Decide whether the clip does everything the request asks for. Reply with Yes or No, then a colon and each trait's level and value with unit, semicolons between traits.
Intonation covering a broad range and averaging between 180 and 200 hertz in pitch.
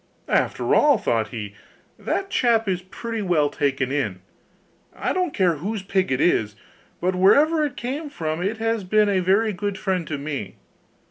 Yes: wide, 7.2 semitones; high, 190 Hz